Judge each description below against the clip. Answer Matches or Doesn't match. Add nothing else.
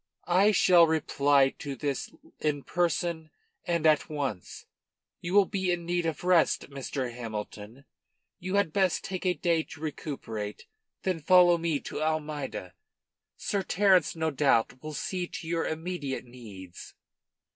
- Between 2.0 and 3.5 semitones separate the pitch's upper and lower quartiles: Doesn't match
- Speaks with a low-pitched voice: Doesn't match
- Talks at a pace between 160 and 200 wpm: Doesn't match